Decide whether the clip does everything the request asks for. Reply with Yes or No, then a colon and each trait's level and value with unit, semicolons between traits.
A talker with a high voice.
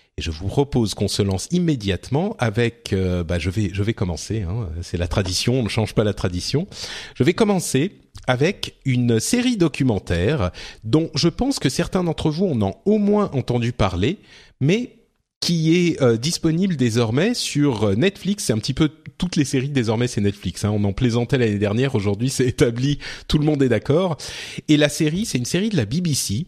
No: low, 130 Hz